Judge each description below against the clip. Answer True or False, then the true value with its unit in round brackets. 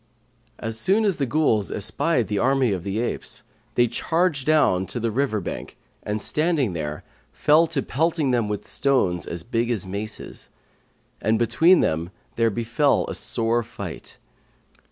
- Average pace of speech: True (155 wpm)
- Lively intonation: True (5.8 semitones)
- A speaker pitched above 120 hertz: False (115 Hz)